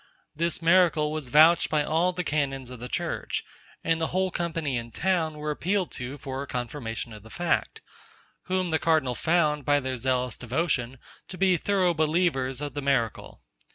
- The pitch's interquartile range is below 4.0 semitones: No, average, 4.6 semitones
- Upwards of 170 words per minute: Yes, average, 180 wpm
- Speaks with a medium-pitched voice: Yes, medium, 150 Hz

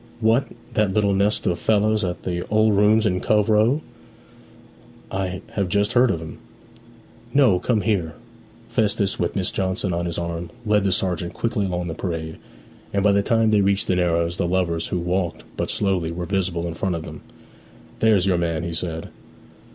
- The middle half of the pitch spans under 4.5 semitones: Yes, average, 3.4 semitones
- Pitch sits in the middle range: No, very low, 95 Hz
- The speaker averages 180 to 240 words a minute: Yes, average, 185 wpm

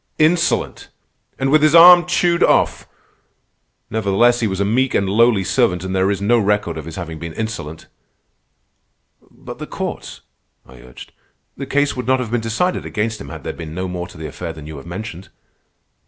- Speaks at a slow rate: No, average, 190 wpm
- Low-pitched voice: Yes, low, 100 Hz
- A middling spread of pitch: No, wide, 6.7 semitones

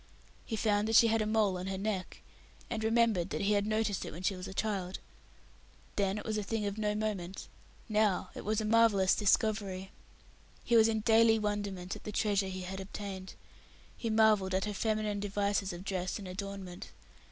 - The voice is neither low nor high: No, high, 205 Hz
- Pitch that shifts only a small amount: Yes, narrow, 2.1 semitones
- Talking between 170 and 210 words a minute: Yes, average, 200 wpm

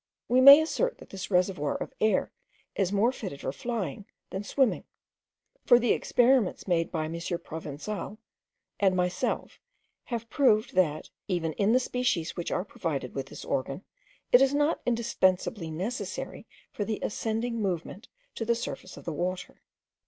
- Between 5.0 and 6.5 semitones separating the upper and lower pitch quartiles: Yes, average, 5.3 semitones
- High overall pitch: Yes, high, 200 Hz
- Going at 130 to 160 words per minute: Yes, average, 155 wpm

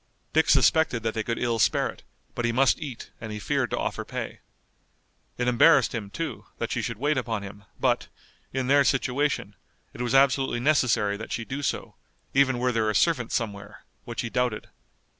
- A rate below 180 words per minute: No, average, 195 wpm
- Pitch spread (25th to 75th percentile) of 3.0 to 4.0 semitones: Yes, average, 3.4 semitones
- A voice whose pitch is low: Yes, low, 125 Hz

